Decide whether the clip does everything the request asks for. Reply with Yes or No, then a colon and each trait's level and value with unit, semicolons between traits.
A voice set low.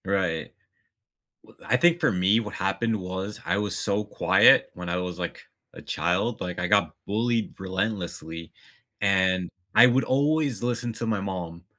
Yes: low, 100 Hz